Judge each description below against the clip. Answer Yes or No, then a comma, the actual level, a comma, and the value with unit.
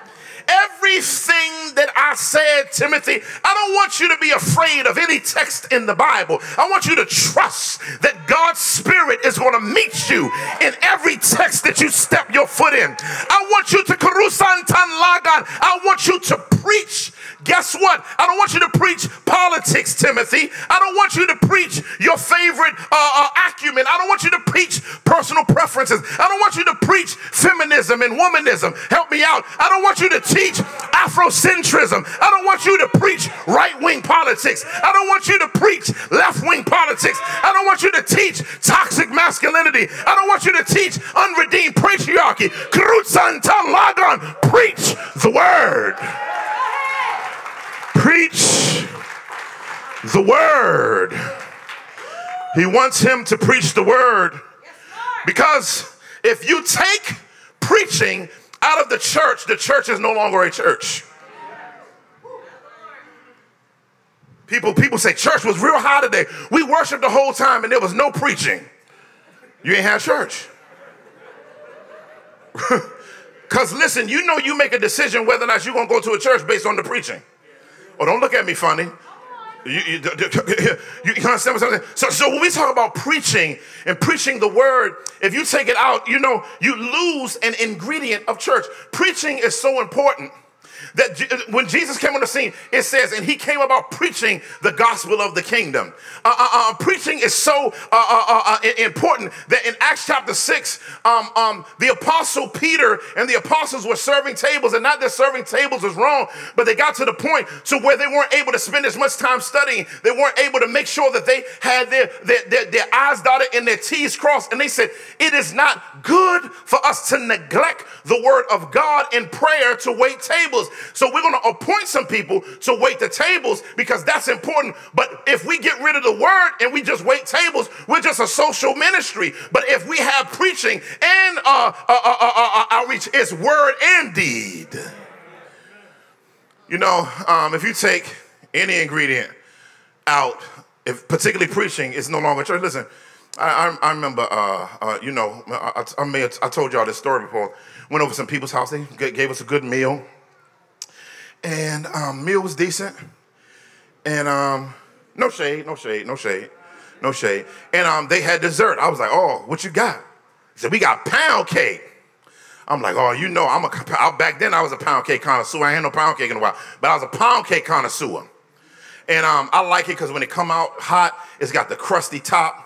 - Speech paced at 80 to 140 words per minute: No, average, 180 wpm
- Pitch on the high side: Yes, very high, 320 Hz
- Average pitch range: No, wide, 8.5 semitones